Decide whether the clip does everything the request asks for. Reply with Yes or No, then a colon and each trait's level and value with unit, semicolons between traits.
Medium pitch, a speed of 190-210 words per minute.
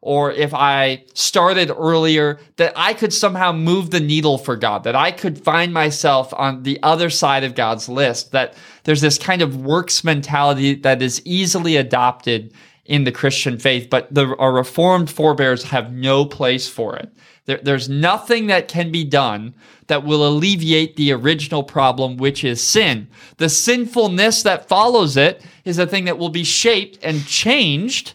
No: medium, 150 Hz; average, 175 wpm